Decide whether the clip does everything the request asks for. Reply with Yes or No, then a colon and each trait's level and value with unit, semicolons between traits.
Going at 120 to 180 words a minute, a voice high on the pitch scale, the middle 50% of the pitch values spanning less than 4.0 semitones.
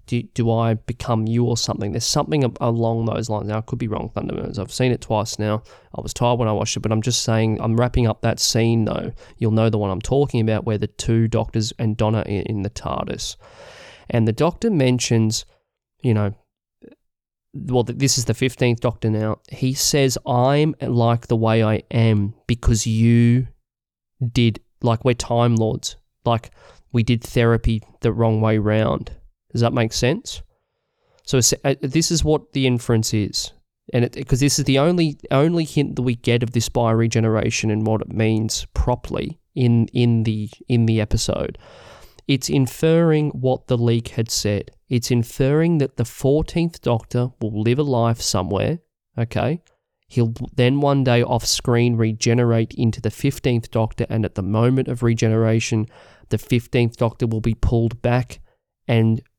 No: average, 175 wpm; low, 115 Hz; narrow, 2.4 semitones